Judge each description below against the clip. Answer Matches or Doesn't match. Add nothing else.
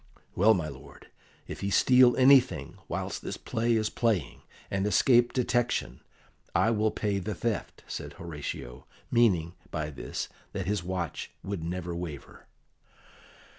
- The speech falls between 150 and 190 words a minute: Doesn't match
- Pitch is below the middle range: Matches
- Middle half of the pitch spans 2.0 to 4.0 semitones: Doesn't match